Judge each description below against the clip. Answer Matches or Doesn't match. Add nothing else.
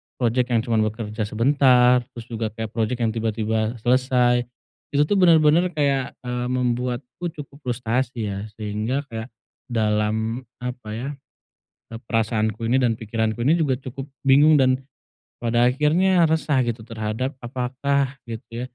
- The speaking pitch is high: Doesn't match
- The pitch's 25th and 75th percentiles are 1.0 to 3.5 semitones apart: Matches